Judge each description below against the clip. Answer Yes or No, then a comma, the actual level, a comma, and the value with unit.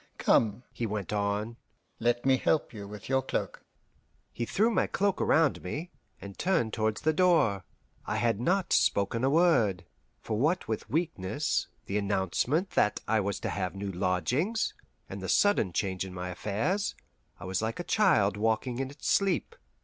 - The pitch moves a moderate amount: No, wide, 7.8 semitones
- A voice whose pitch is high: No, low, 115 Hz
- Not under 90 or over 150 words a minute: No, average, 170 wpm